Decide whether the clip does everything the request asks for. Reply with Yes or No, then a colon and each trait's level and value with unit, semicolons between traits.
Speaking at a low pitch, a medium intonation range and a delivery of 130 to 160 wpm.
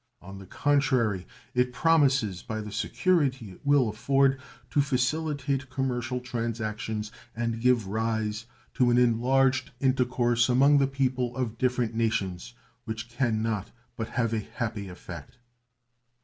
Yes: low, 120 Hz; average, 3.1 semitones; slow, 135 wpm